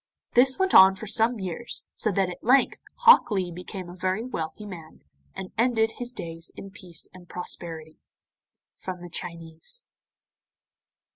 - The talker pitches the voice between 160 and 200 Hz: Yes, high, 190 Hz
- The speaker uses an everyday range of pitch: Yes, average, 4.8 semitones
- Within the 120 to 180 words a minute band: Yes, average, 150 wpm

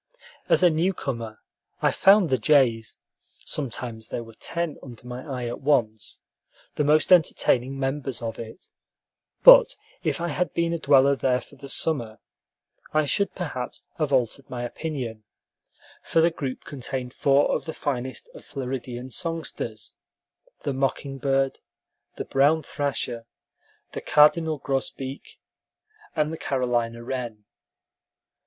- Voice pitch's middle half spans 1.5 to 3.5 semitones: No, average, 3.9 semitones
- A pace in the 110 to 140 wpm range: Yes, slow, 135 wpm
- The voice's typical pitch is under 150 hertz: Yes, low, 135 Hz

